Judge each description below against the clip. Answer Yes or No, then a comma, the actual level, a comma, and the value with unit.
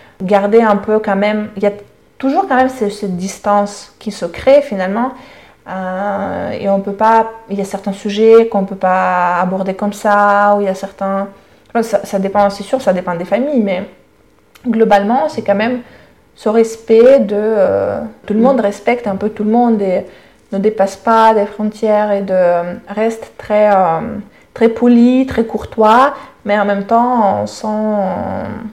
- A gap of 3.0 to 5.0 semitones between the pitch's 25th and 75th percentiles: No, narrow, 2.4 semitones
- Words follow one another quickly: No, average, 185 wpm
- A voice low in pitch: No, high, 210 Hz